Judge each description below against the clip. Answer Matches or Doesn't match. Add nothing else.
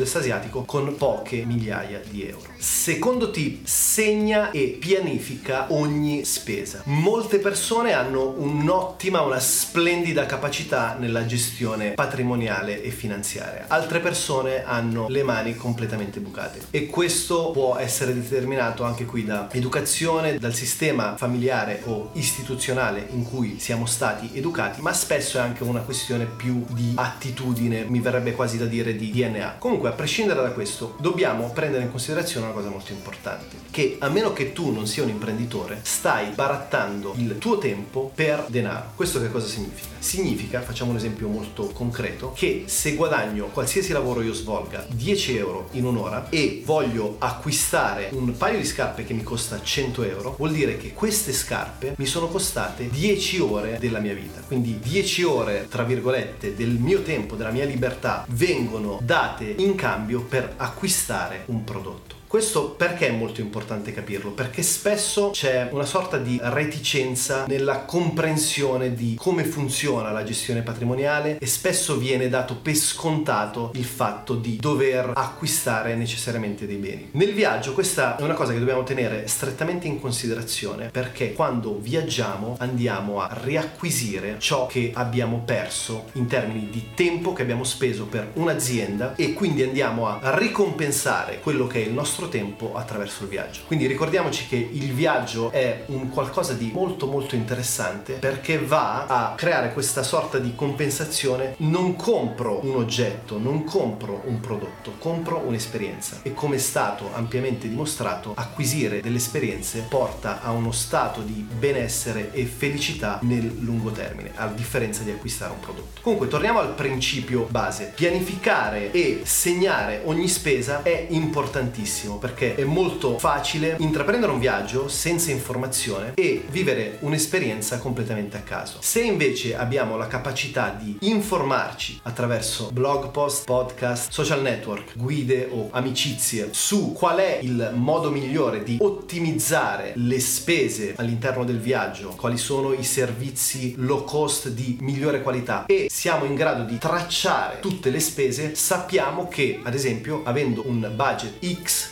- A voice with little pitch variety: Doesn't match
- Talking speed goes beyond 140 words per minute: Matches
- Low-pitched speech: Matches